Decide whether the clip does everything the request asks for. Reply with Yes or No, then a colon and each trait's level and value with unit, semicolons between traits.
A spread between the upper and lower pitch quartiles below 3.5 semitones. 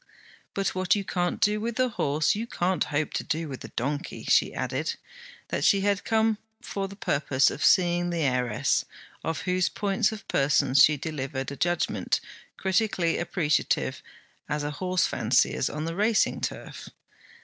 No: average, 5.2 semitones